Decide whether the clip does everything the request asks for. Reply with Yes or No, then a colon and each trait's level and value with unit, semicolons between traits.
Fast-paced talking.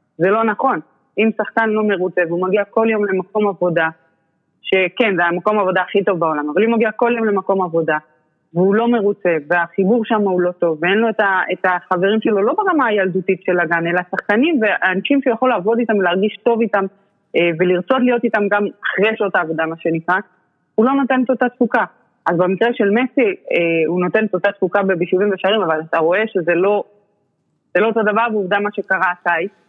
Yes: fast, 190 wpm